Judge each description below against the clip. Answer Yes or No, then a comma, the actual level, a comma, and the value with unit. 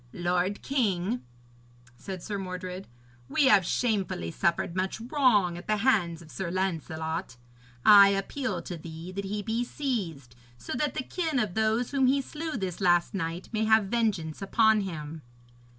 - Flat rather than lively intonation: No, average, 4.6 semitones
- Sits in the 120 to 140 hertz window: No, high, 195 Hz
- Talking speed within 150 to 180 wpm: Yes, average, 160 wpm